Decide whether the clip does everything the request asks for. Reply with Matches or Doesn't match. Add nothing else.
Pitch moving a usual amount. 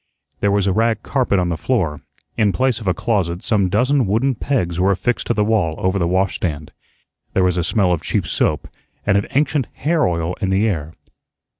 Matches